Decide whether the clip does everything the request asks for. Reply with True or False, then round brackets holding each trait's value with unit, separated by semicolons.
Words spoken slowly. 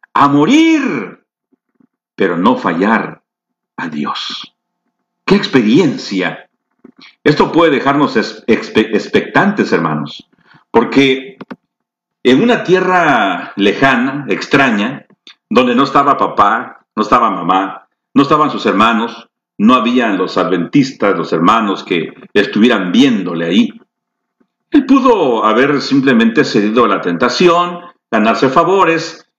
True (105 wpm)